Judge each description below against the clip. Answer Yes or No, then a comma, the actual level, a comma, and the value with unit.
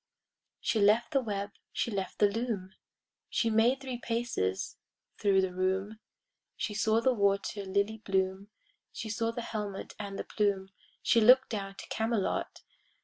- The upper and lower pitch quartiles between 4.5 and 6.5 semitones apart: No, average, 2.7 semitones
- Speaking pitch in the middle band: No, high, 210 Hz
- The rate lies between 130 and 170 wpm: Yes, average, 150 wpm